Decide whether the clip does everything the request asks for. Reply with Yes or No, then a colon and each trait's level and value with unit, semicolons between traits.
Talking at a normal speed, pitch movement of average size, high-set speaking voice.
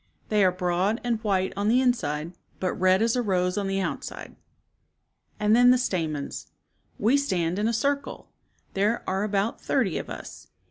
Yes: average, 180 wpm; average, 4.0 semitones; high, 200 Hz